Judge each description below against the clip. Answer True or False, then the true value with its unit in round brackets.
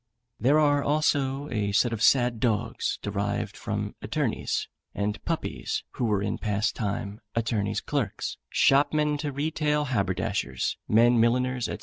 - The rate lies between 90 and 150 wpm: True (135 wpm)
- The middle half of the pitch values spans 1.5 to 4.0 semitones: False (5.3 semitones)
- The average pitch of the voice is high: False (115 Hz)